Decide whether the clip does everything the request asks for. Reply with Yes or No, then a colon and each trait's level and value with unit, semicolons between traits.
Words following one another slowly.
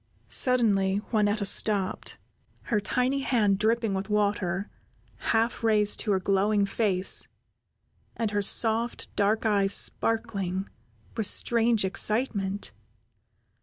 Yes: slow, 105 wpm